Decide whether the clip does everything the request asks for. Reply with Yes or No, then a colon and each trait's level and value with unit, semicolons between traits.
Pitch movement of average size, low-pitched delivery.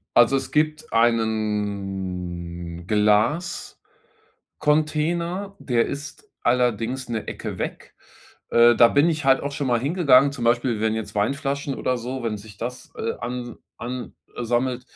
Yes: average, 4.0 semitones; low, 120 Hz